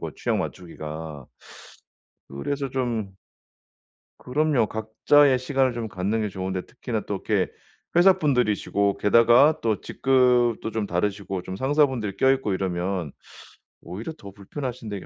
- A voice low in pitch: Yes, low, 110 Hz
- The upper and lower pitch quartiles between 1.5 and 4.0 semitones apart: No, wide, 5.4 semitones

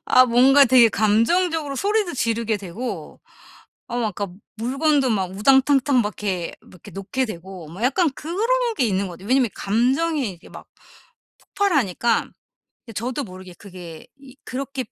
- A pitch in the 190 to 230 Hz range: No, high, 240 Hz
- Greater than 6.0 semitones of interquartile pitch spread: No, wide, 5.7 semitones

